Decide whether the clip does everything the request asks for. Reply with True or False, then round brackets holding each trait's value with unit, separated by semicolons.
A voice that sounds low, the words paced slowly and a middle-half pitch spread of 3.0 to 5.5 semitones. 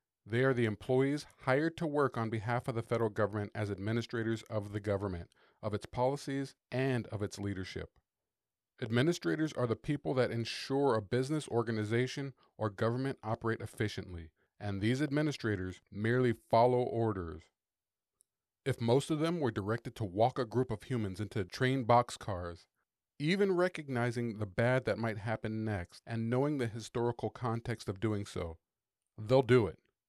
False (115 Hz; 155 wpm; 3.4 semitones)